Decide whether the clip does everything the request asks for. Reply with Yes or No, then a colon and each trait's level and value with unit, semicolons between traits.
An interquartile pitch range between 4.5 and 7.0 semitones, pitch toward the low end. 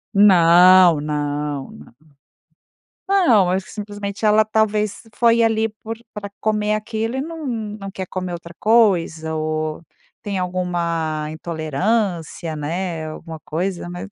No: average, 4.9 semitones; medium, 185 Hz